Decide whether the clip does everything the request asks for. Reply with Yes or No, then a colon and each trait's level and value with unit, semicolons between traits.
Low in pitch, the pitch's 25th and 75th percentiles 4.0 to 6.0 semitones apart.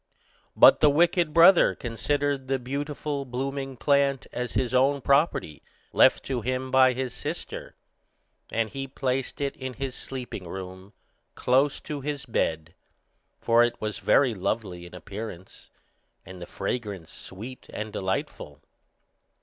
Yes: low, 130 Hz; average, 4.4 semitones